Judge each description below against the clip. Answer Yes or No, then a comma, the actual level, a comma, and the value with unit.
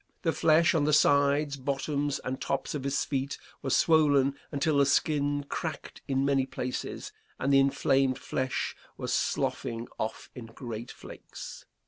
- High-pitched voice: No, medium, 140 Hz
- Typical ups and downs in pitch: No, narrow, 1.6 semitones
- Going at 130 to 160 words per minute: Yes, average, 150 wpm